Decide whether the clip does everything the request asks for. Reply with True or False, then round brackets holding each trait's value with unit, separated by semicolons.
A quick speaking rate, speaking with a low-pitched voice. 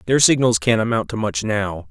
True (220 wpm; 105 Hz)